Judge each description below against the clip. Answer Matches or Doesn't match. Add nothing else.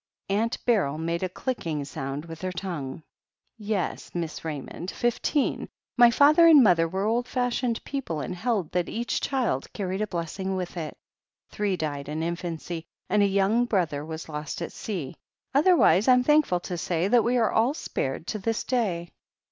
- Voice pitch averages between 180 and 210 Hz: Matches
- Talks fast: Doesn't match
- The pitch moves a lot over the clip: Matches